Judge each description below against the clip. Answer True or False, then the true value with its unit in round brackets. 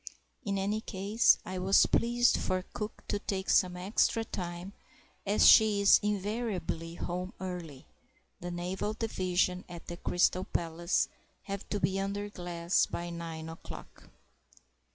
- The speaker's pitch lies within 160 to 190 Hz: True (185 Hz)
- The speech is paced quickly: False (135 wpm)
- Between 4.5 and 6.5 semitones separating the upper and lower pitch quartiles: False (2.8 semitones)